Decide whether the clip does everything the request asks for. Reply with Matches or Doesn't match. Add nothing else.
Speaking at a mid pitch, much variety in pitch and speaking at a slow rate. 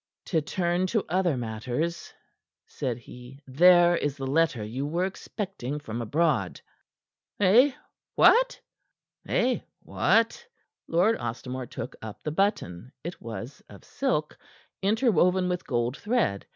Matches